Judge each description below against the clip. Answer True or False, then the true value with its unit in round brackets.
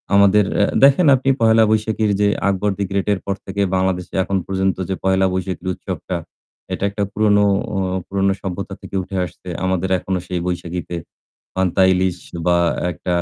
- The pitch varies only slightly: True (1.7 semitones)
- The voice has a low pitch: True (95 Hz)